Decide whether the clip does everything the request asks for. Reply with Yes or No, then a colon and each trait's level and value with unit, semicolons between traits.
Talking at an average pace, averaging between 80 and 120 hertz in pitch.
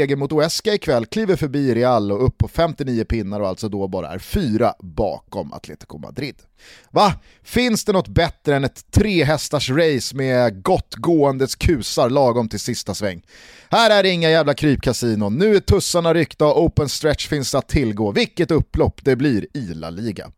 No: average, 180 wpm; medium, 140 Hz